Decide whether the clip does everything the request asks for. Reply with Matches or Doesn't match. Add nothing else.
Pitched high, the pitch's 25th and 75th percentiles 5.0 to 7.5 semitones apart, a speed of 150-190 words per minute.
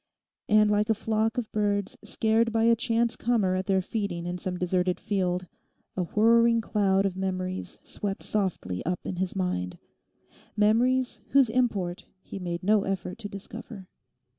Doesn't match